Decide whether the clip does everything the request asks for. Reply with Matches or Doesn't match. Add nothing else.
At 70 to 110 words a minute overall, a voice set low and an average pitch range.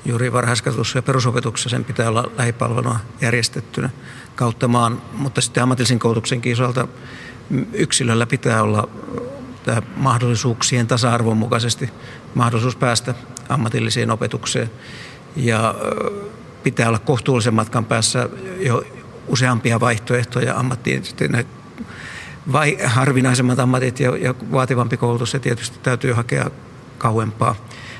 Doesn't match